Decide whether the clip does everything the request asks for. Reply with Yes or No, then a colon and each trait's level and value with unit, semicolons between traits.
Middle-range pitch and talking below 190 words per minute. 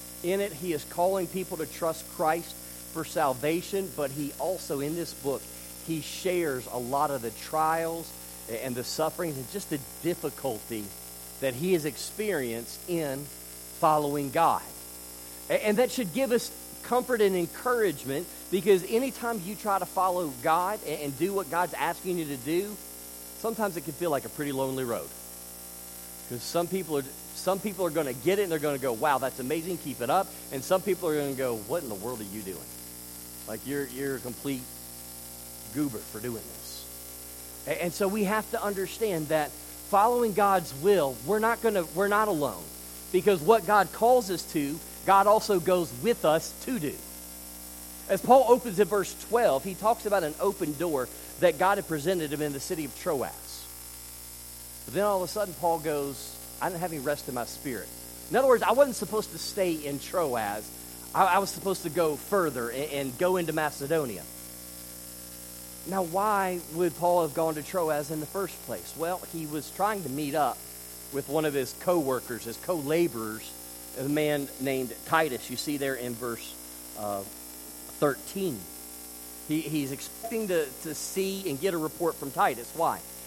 Yes: medium, 150 Hz; average, 180 wpm